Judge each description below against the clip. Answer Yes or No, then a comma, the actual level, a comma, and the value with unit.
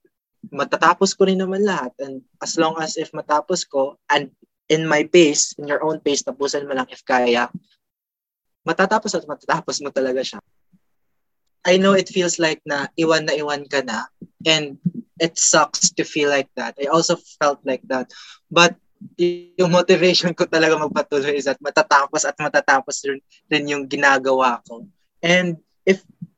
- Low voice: No, medium, 155 Hz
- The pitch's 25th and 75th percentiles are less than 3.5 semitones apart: No, average, 4.0 semitones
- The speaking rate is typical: Yes, average, 160 wpm